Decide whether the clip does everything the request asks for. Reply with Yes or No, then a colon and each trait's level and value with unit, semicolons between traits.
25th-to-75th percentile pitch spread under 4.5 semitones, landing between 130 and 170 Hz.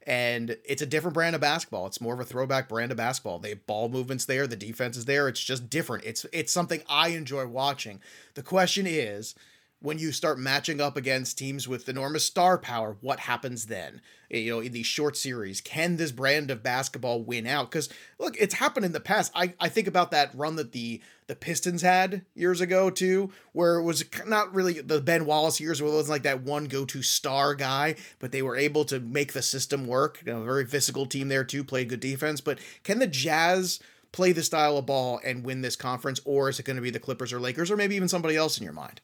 Yes: average, 4.0 semitones; medium, 140 Hz